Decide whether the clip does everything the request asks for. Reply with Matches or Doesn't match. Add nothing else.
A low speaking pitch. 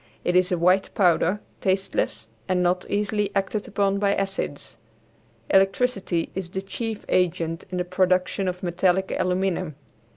Doesn't match